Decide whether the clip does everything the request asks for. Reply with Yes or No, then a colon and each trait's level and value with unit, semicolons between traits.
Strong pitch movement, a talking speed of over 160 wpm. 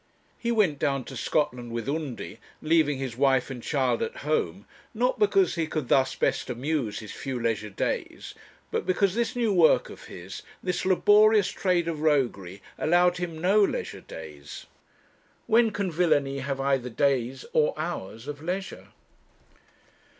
No: wide, 6.1 semitones; average, 155 wpm